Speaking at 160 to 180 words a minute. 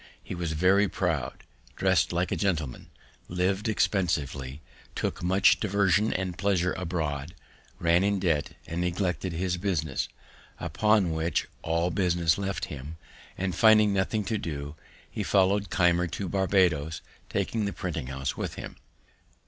No: average, 140 wpm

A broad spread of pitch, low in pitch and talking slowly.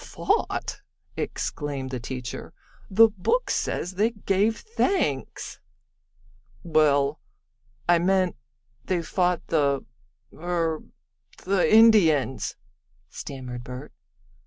No: wide, 6.0 semitones; medium, 170 Hz; slow, 85 wpm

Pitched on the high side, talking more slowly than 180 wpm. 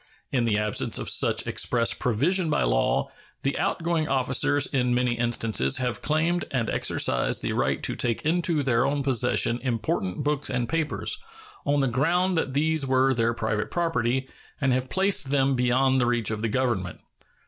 No: low, 130 Hz; average, 170 wpm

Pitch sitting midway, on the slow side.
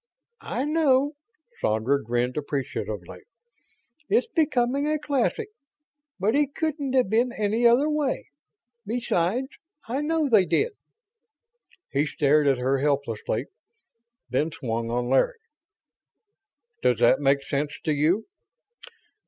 No: high, 210 Hz; slow, 115 wpm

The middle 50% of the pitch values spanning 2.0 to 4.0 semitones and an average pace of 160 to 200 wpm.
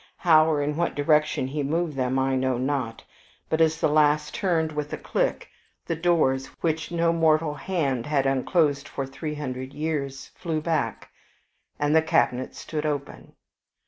Yes: average, 2.9 semitones; average, 165 wpm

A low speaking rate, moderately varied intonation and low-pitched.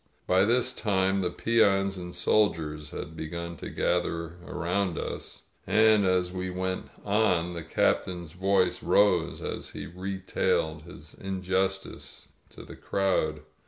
No: slow, 130 wpm; narrow, 2.2 semitones; very low, 90 Hz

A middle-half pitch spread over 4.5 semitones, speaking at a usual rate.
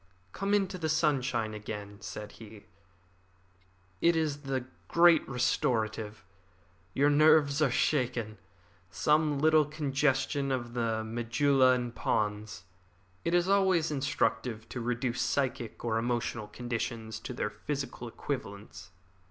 No: average, 4.9 semitones; slow, 120 wpm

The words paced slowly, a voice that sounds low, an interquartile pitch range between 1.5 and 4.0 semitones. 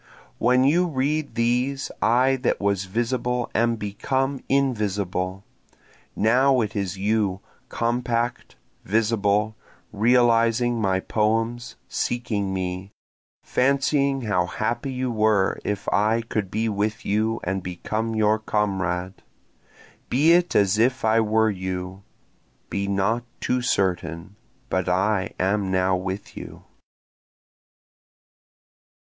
Yes: slow, 115 wpm; low, 110 Hz; average, 3.7 semitones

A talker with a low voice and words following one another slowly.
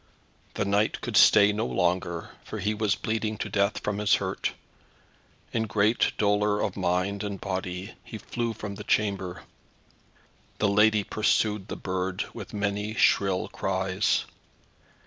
No: low, 100 Hz; average, 145 wpm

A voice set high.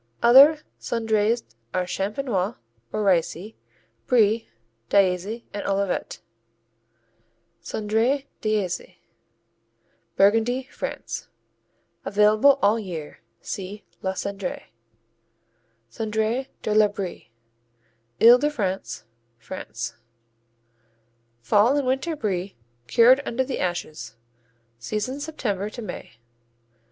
Yes: high, 210 Hz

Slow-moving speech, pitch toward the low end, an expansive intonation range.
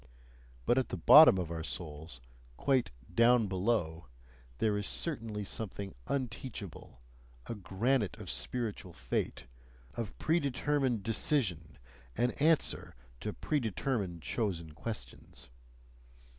Yes: slow, 105 wpm; low, 105 Hz; wide, 6.2 semitones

